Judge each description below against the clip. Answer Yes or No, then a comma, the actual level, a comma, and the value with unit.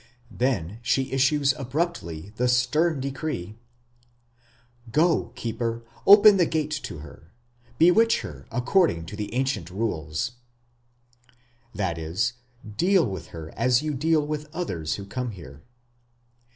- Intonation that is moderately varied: No, wide, 8.4 semitones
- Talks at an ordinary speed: No, slow, 125 wpm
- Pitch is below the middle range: Yes, low, 125 Hz